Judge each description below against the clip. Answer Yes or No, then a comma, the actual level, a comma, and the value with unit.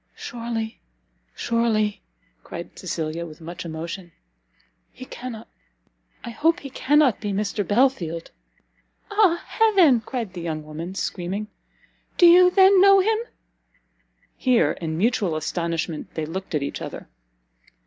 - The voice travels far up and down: Yes, wide, 8.2 semitones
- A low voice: No, high, 215 Hz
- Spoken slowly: Yes, slow, 125 wpm